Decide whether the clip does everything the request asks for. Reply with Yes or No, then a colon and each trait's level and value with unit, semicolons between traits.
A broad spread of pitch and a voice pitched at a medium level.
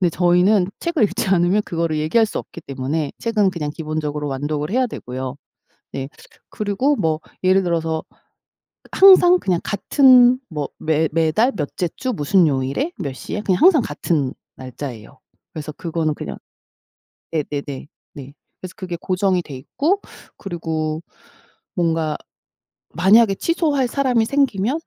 Yes: wide, 6.2 semitones; medium, 170 Hz